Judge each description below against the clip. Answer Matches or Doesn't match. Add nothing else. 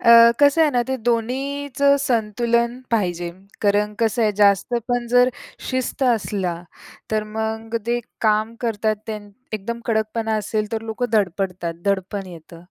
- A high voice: Matches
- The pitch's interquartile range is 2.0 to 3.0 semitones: Matches